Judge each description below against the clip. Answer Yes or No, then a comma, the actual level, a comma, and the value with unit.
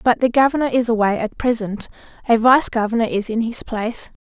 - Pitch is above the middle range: Yes, high, 230 Hz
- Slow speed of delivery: No, average, 200 wpm